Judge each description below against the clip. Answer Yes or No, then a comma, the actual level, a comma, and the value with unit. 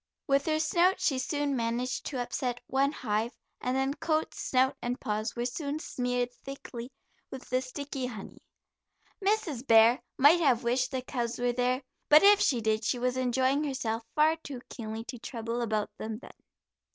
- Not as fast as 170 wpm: No, average, 175 wpm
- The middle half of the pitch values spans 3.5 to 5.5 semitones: No, average, 2.9 semitones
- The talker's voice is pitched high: Yes, very high, 255 Hz